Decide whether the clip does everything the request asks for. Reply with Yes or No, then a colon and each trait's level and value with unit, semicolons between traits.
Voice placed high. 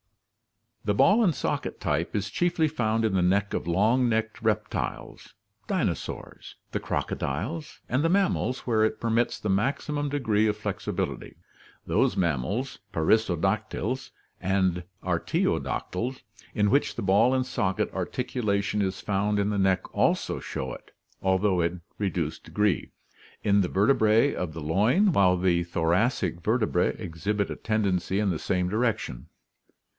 No: low, 105 Hz